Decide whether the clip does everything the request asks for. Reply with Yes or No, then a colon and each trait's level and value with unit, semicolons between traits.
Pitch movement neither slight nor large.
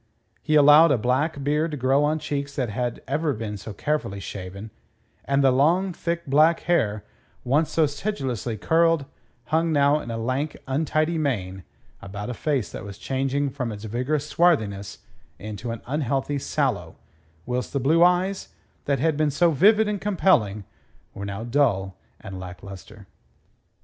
No: wide, 5.7 semitones